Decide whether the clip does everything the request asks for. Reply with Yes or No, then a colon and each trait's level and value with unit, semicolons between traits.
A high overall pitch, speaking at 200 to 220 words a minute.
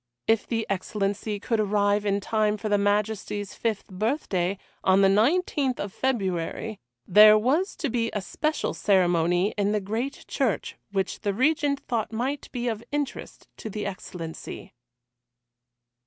No: high, 210 Hz; average, 145 wpm